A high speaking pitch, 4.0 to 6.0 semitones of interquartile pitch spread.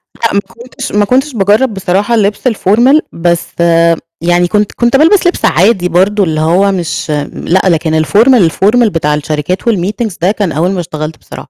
Yes: high, 195 Hz; average, 4.9 semitones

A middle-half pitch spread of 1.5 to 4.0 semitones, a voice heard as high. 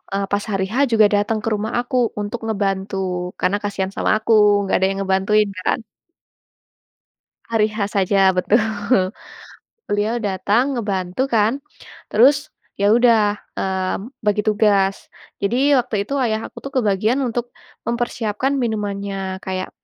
Yes: average, 3.0 semitones; high, 210 Hz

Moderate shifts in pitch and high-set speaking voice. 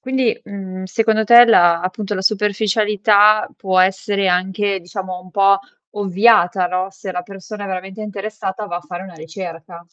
No: narrow, 2.3 semitones; high, 195 Hz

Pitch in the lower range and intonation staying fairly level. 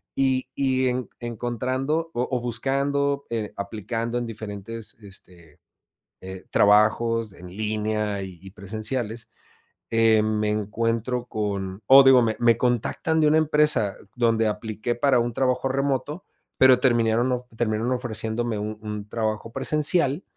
No: low, 115 Hz; average, 3.2 semitones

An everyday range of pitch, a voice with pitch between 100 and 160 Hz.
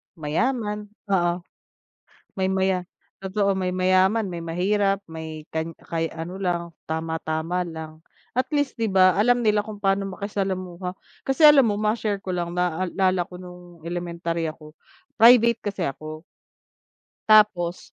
No: average, 3.3 semitones; medium, 185 Hz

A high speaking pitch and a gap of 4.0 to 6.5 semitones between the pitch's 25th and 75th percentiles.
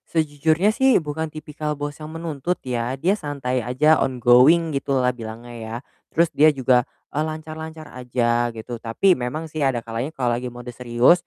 No: medium, 140 Hz; average, 4.4 semitones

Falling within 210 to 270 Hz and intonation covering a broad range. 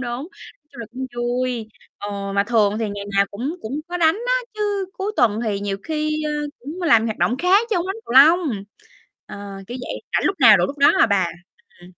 Yes: very high, 250 Hz; wide, 7.1 semitones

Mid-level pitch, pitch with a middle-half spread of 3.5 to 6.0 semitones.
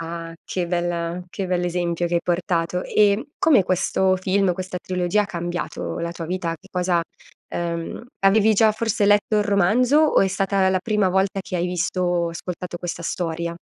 No: medium, 180 Hz; narrow, 2.5 semitones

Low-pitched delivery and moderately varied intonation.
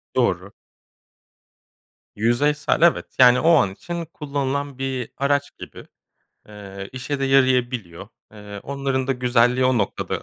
Yes: low, 130 Hz; average, 3.2 semitones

